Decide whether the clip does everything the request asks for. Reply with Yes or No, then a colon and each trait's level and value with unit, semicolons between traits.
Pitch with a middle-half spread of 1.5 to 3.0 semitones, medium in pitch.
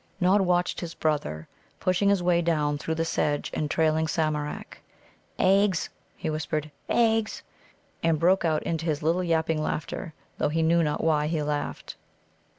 Yes: narrow, 2.5 semitones; medium, 160 Hz